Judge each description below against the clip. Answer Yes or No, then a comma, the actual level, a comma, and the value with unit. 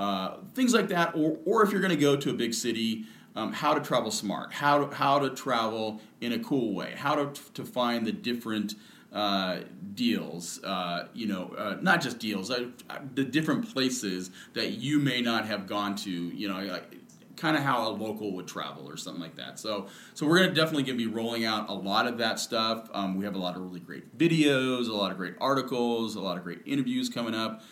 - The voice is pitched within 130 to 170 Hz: No, low, 115 Hz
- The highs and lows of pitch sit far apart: Yes, wide, 5.7 semitones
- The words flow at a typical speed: No, fast, 225 wpm